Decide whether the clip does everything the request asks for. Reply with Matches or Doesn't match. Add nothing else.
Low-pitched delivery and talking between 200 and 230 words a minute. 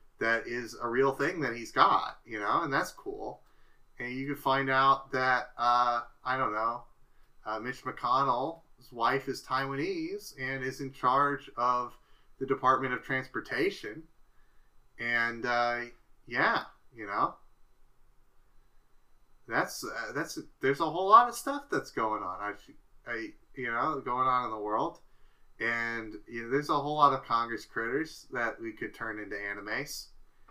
Doesn't match